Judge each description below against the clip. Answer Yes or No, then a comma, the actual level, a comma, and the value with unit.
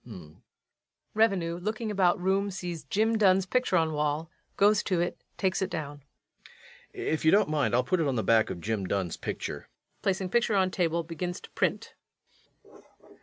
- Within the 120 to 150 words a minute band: No, average, 170 wpm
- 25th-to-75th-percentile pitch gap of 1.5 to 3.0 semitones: No, average, 4.3 semitones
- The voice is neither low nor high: Yes, medium, 180 Hz